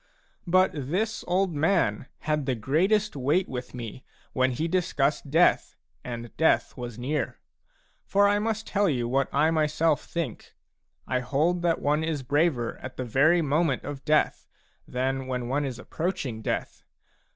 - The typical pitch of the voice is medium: Yes, medium, 145 Hz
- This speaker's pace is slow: No, average, 155 wpm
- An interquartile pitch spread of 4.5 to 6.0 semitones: Yes, average, 4.9 semitones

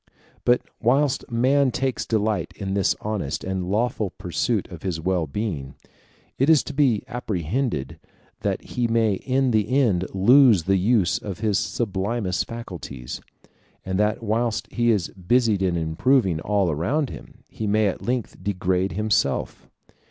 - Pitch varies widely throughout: No, average, 4.6 semitones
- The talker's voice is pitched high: No, low, 105 Hz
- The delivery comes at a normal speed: Yes, average, 145 wpm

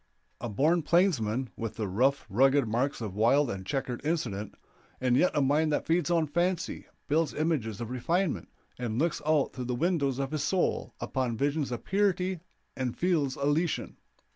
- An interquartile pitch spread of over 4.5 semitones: Yes, average, 5.2 semitones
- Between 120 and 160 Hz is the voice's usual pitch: Yes, medium, 140 Hz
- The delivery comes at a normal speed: Yes, average, 170 wpm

